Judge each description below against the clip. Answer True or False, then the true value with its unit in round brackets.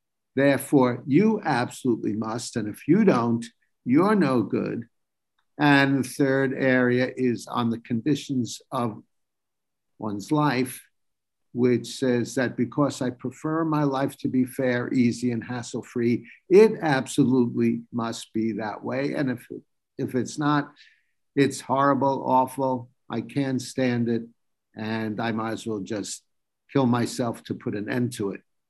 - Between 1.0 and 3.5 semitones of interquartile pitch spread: True (2.7 semitones)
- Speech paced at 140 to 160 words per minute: True (145 wpm)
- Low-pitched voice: True (125 Hz)